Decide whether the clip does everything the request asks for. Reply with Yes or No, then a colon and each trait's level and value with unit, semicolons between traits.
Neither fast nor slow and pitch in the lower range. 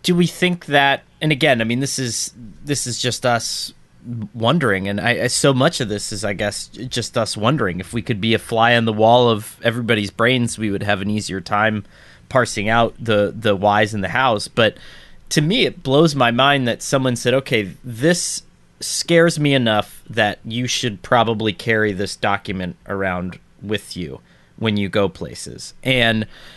Yes: average, 185 wpm; low, 115 Hz